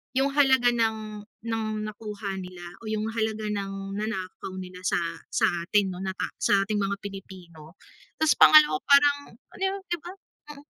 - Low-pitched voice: No, high, 210 Hz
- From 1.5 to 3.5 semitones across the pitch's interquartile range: No, average, 3.9 semitones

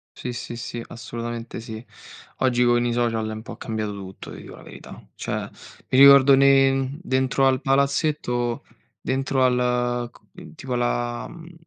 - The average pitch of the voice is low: Yes, low, 125 Hz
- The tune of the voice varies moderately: No, narrow, 2.3 semitones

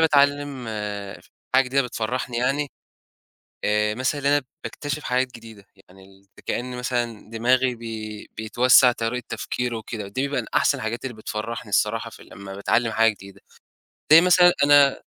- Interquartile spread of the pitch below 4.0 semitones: Yes, average, 3.5 semitones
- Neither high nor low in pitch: No, low, 120 Hz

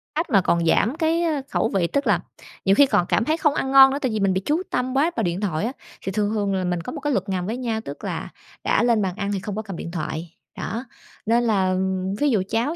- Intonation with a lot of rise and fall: Yes, wide, 6.1 semitones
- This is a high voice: Yes, high, 215 Hz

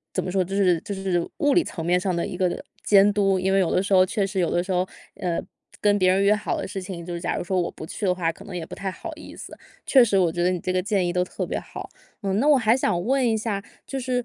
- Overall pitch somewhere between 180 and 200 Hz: Yes, high, 190 Hz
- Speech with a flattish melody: Yes, narrow, 2.3 semitones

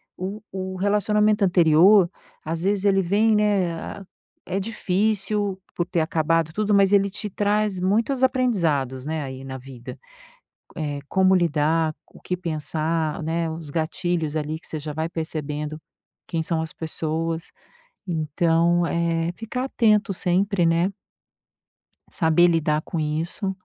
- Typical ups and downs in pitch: Yes, average, 3.9 semitones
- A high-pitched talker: No, medium, 170 Hz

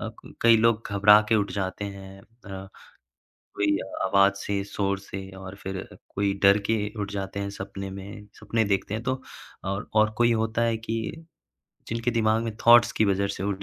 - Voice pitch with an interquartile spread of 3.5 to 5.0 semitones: No, narrow, 2.4 semitones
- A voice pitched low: Yes, low, 100 Hz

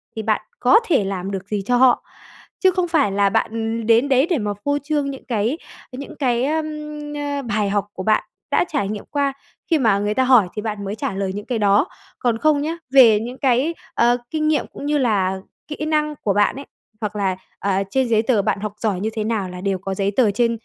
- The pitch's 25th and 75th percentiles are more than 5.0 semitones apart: Yes, wide, 5.5 semitones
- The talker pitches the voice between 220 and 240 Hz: Yes, high, 230 Hz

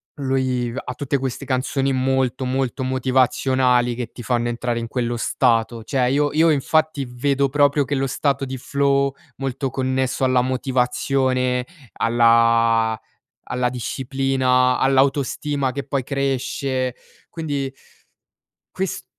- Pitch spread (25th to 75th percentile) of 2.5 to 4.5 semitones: No, narrow, 1.7 semitones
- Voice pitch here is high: No, low, 130 Hz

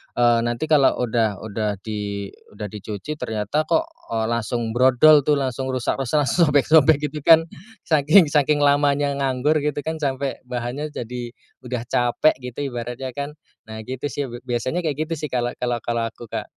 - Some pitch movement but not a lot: Yes, average, 3.9 semitones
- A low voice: Yes, low, 130 Hz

